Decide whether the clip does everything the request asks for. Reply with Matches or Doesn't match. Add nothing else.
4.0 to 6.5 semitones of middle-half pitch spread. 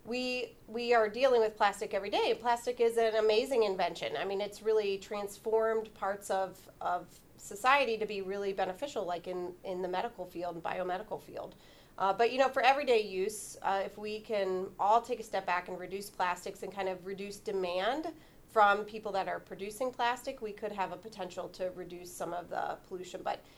Doesn't match